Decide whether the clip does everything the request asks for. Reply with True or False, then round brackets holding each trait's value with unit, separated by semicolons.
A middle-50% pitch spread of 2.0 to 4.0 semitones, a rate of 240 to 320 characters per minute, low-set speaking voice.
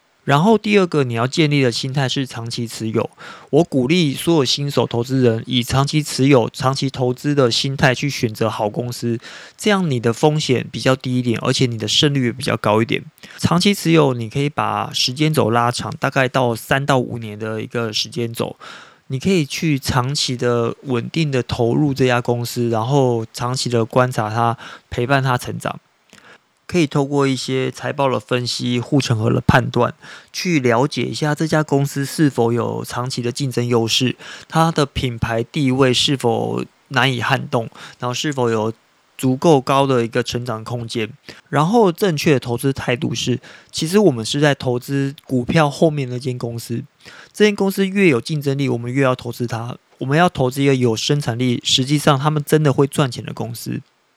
True (3.5 semitones; 280 characters per minute; 130 Hz)